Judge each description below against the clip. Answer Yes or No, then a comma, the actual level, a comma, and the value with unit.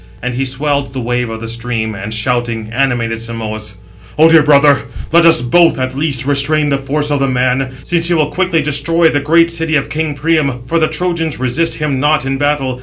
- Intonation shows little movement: No, average, 4.0 semitones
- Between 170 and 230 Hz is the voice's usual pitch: No, medium, 140 Hz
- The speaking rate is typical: No, fast, 210 wpm